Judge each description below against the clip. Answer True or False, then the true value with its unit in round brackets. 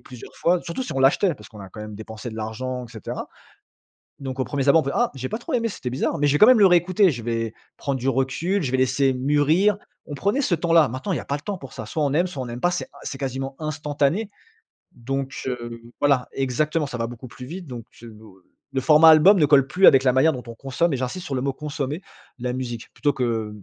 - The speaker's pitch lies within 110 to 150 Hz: True (135 Hz)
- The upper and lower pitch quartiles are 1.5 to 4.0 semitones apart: False (4.5 semitones)